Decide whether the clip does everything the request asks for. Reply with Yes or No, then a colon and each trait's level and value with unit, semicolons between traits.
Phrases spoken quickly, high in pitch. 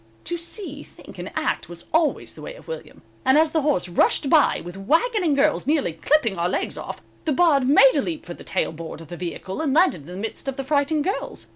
Yes: fast, 245 wpm; very high, 280 Hz